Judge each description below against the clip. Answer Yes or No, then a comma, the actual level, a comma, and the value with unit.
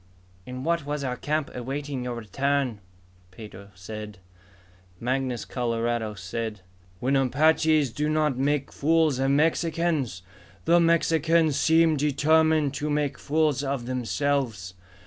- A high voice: No, medium, 140 Hz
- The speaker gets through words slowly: Yes, slow, 120 wpm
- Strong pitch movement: No, average, 4.3 semitones